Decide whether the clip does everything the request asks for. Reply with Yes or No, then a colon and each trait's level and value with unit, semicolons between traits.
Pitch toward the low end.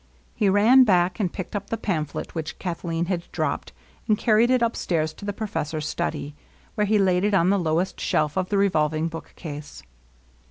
No: medium, 185 Hz